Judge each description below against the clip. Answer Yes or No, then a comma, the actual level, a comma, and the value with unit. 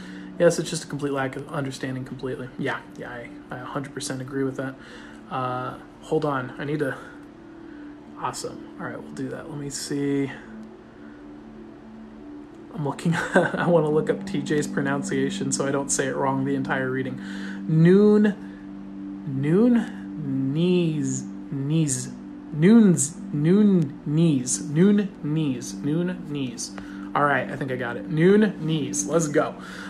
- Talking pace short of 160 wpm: Yes, average, 145 wpm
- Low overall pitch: No, medium, 145 Hz